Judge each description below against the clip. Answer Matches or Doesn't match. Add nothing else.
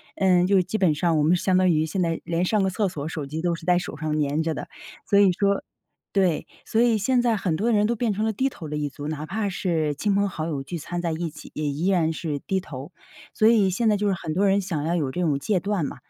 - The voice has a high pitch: Doesn't match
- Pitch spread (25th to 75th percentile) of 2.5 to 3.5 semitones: Doesn't match